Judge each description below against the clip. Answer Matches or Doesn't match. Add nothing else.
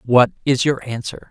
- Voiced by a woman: Doesn't match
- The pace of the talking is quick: Doesn't match